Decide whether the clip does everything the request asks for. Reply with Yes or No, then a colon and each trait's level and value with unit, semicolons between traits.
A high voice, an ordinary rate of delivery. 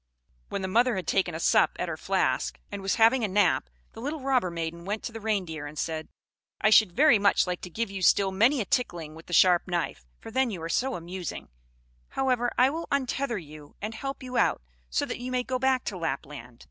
No: high, 200 Hz; fast, 230 wpm